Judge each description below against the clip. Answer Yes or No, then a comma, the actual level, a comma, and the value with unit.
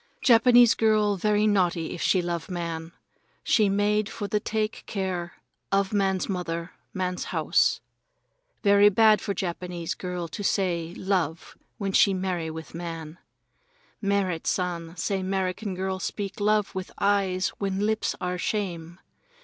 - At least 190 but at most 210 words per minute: No, average, 140 wpm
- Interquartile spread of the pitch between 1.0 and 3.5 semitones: Yes, average, 2.8 semitones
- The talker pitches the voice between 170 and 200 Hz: Yes, high, 190 Hz